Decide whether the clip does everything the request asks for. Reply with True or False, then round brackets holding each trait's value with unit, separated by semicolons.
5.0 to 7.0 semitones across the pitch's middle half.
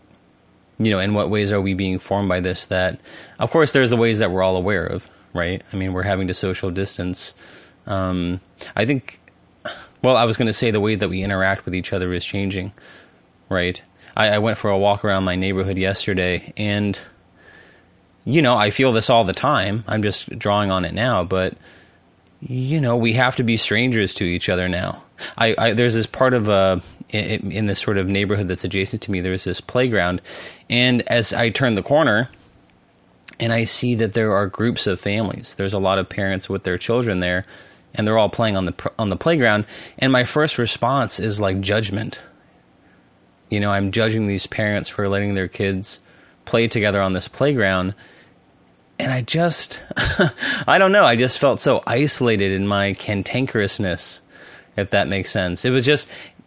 False (3.4 semitones)